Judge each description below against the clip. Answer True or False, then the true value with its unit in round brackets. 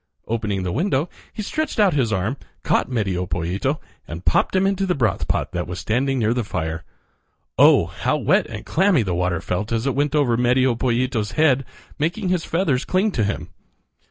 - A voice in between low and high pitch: False (125 Hz)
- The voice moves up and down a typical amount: False (7.5 semitones)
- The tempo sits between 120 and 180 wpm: False (190 wpm)